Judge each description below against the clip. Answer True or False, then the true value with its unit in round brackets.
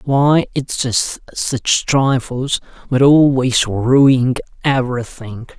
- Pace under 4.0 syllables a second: True (3.0 syllables/s)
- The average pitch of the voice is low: True (130 Hz)